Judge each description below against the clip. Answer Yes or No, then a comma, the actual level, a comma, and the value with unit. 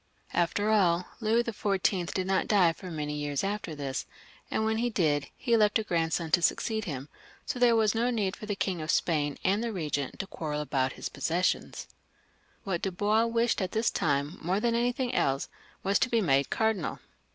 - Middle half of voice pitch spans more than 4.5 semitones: Yes, wide, 5.6 semitones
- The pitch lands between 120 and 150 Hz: No, high, 190 Hz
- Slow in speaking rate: No, average, 195 wpm